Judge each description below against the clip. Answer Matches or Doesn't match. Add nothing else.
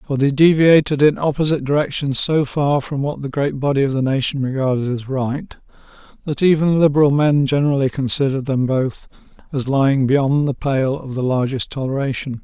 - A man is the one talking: Matches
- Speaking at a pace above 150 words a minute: Matches